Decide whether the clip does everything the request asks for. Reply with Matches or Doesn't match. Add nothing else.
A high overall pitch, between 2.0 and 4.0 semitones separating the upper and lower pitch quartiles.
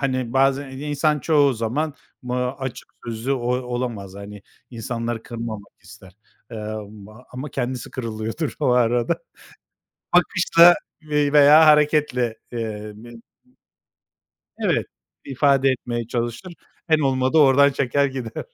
Doesn't match